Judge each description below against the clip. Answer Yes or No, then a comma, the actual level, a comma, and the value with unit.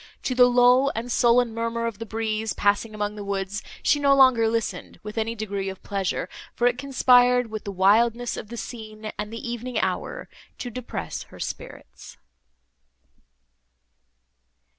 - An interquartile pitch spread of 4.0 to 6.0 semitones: No, narrow, 2.6 semitones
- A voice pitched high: Yes, high, 230 Hz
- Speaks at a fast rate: No, average, 160 wpm